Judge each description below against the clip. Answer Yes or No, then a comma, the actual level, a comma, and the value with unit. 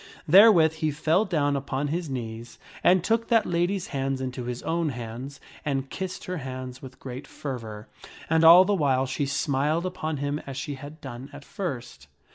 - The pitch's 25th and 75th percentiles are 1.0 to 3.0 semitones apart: No, average, 4.2 semitones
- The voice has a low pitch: No, medium, 145 Hz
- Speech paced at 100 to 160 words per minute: No, average, 180 wpm